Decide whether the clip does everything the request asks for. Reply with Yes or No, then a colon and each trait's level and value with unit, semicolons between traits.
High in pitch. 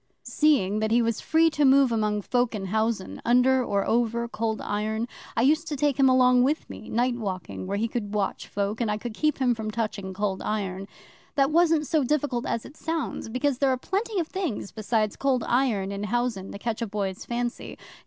Yes: high, 235 Hz